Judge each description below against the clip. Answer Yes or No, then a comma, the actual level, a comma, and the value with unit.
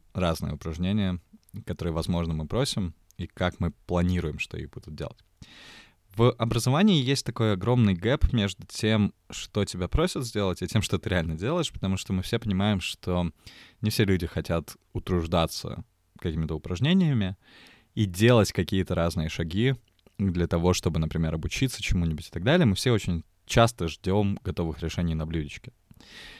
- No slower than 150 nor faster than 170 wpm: Yes, average, 155 wpm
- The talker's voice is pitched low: Yes, very low, 95 Hz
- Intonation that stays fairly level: No, average, 4.6 semitones